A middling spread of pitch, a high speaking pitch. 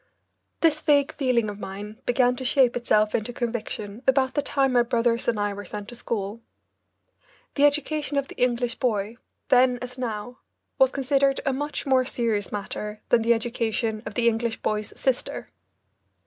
Yes: average, 3.4 semitones; high, 240 Hz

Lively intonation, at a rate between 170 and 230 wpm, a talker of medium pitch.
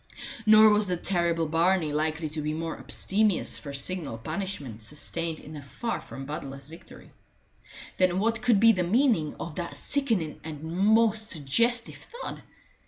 No: wide, 5.9 semitones; average, 155 wpm; medium, 170 Hz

